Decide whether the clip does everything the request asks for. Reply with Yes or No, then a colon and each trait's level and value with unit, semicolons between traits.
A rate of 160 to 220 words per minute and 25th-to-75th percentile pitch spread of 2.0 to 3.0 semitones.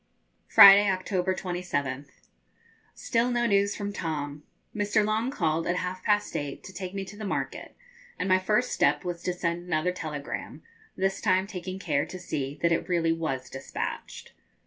No: average, 170 wpm; average, 3.6 semitones